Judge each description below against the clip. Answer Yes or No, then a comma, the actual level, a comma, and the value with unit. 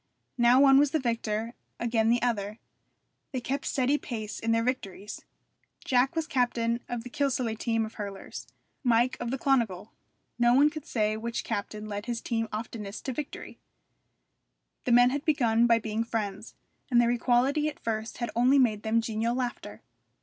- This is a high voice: Yes, high, 235 Hz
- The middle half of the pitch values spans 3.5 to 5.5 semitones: No, narrow, 2.4 semitones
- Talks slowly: No, average, 170 wpm